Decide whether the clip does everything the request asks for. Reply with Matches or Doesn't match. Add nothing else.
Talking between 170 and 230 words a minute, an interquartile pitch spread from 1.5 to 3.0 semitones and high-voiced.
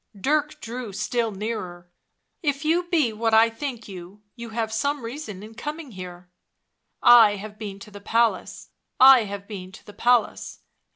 Doesn't match